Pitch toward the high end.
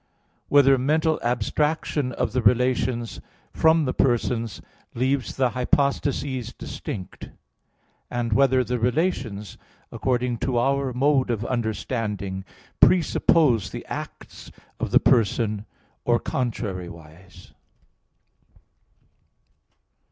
No: low, 125 Hz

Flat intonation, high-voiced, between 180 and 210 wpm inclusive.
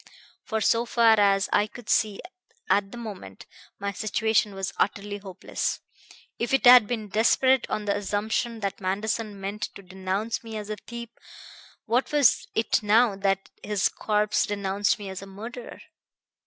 No: narrow, 2.3 semitones; high, 210 Hz; average, 160 wpm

